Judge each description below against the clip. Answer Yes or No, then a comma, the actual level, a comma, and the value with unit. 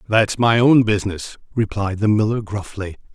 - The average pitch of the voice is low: Yes, low, 105 Hz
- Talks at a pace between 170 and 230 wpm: No, average, 150 wpm